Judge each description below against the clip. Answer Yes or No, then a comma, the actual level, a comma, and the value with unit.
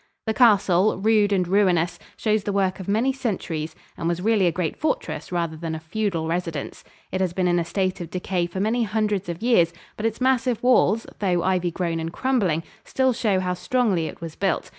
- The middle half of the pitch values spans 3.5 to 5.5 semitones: Yes, average, 4.1 semitones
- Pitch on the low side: No, high, 190 Hz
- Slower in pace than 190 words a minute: No, fast, 205 wpm